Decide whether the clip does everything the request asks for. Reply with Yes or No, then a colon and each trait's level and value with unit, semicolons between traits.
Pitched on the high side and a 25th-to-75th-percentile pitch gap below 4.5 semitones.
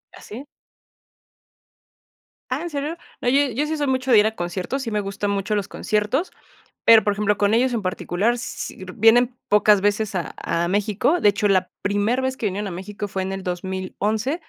Yes: high, 210 Hz; average, 4.1 semitones